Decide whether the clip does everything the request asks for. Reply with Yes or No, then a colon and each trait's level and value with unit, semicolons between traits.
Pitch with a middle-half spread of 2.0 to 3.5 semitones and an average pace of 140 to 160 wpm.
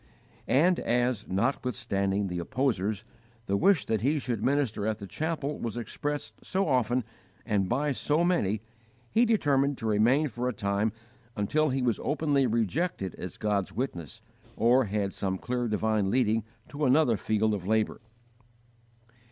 No: average, 5.2 semitones; average, 150 wpm